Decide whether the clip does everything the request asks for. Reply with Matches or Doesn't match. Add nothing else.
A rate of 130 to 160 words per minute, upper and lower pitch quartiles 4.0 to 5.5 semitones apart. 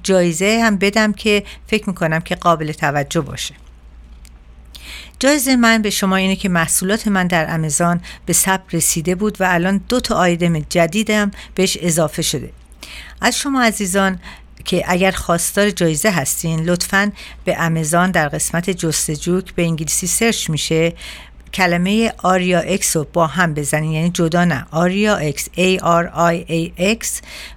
Doesn't match